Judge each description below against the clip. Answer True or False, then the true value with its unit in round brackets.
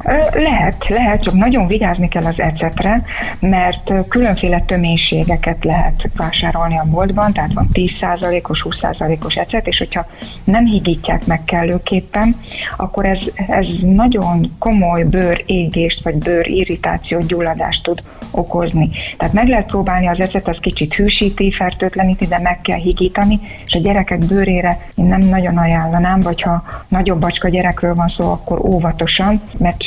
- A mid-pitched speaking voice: True (180 Hz)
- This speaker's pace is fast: False (145 wpm)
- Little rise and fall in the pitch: True (2.3 semitones)